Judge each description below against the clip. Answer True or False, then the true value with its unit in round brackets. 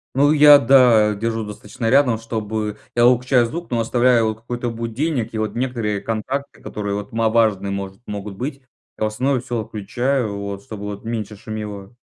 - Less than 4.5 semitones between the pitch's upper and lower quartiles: True (2.9 semitones)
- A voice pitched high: False (115 Hz)